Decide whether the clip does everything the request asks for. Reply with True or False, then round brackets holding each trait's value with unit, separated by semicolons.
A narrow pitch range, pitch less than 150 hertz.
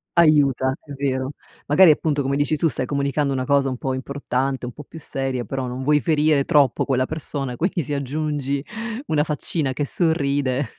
True (2.1 semitones; 140 Hz)